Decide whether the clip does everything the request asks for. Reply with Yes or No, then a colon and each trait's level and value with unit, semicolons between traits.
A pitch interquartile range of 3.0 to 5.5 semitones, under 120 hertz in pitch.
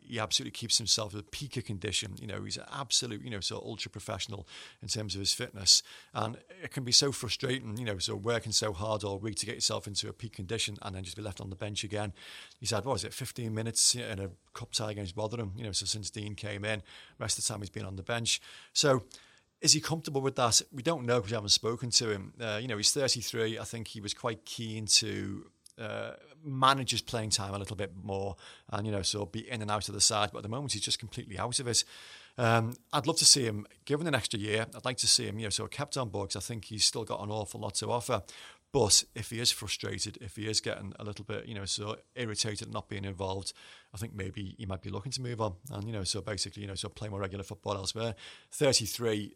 No: narrow, 2.4 semitones; low, 110 Hz